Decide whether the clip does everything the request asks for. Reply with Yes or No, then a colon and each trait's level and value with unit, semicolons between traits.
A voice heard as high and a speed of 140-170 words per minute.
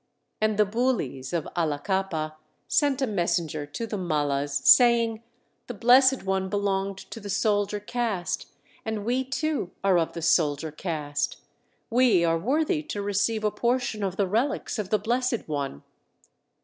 Yes: high, 205 Hz; average, 150 wpm